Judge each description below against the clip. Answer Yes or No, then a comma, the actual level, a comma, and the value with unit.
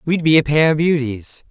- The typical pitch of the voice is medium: Yes, medium, 150 Hz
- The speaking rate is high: Yes, fast, 240 wpm